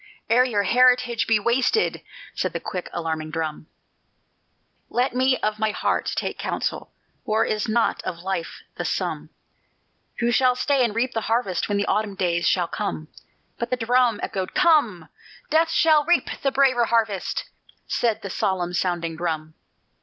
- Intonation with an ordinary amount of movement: No, wide, 5.7 semitones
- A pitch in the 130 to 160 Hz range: No, high, 220 Hz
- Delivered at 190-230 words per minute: No, average, 160 wpm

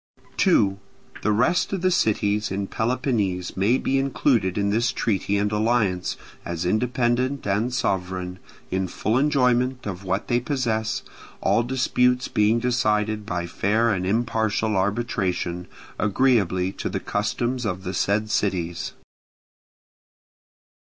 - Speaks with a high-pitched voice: No, low, 110 Hz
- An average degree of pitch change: Yes, average, 4.3 semitones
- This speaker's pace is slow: Yes, slow, 125 wpm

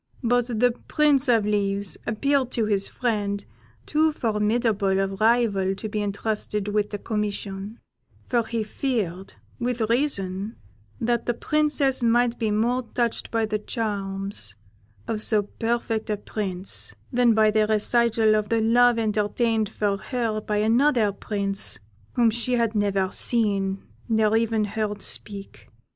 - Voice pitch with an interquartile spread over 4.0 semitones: No, narrow, 2.5 semitones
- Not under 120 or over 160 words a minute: Yes, average, 140 wpm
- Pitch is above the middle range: Yes, high, 220 Hz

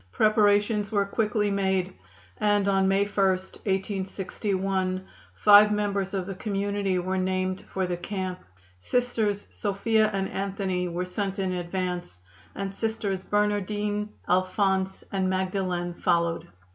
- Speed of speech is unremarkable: No, slow, 120 wpm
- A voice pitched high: Yes, high, 195 Hz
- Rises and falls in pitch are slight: Yes, narrow, 1.7 semitones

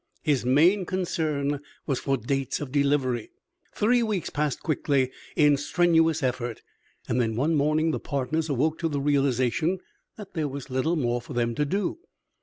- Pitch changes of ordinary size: Yes, average, 3.8 semitones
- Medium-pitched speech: Yes, medium, 145 Hz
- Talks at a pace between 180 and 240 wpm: No, average, 165 wpm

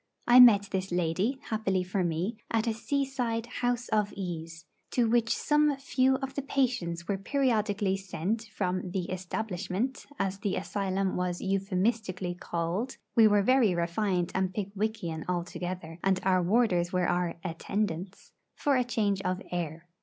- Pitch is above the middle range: Yes, high, 195 Hz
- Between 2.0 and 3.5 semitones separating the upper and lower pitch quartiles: No, average, 4.2 semitones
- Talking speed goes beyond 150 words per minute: No, average, 145 wpm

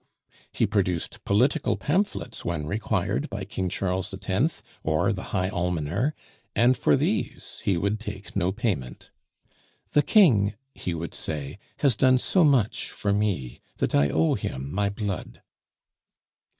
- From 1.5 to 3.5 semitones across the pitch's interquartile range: No, average, 4.7 semitones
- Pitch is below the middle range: Yes, low, 100 Hz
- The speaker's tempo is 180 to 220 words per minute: No, average, 140 wpm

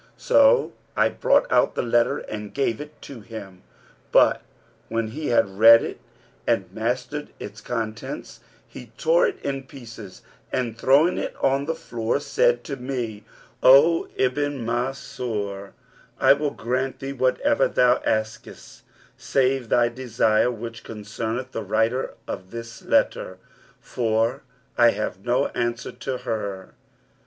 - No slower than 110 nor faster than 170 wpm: Yes, slow, 135 wpm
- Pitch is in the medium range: No, low, 120 Hz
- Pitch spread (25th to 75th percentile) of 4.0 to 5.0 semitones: No, average, 3.4 semitones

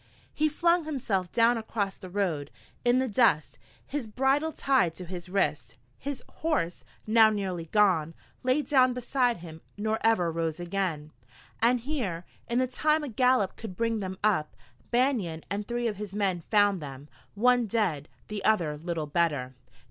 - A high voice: Yes, high, 210 Hz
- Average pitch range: No, wide, 6.2 semitones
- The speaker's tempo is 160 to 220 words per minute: Yes, average, 165 wpm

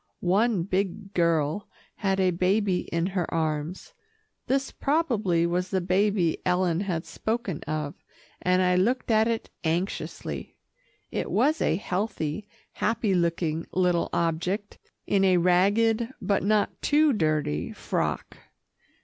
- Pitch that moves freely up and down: No, average, 3.7 semitones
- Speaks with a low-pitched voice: No, medium, 185 Hz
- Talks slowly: Yes, slow, 125 wpm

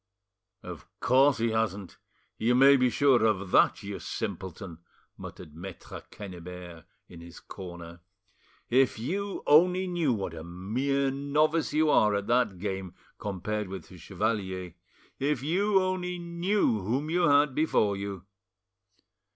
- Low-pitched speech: Yes, low, 115 Hz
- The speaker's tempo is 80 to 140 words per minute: Yes, slow, 135 wpm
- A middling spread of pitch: No, wide, 7.7 semitones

